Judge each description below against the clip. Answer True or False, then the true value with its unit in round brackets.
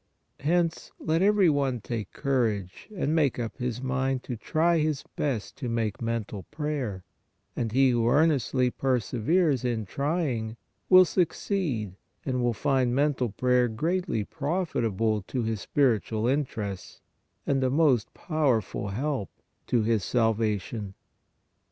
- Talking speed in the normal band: False (125 wpm)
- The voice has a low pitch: True (125 Hz)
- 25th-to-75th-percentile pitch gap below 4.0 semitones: False (4.9 semitones)